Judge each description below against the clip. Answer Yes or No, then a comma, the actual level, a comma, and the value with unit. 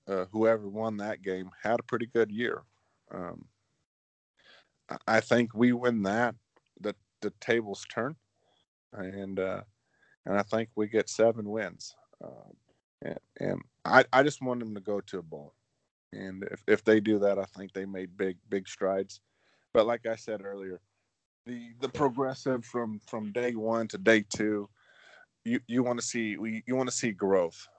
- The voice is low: Yes, low, 110 Hz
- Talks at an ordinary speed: Yes, average, 175 wpm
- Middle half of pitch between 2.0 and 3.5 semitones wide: Yes, average, 3.2 semitones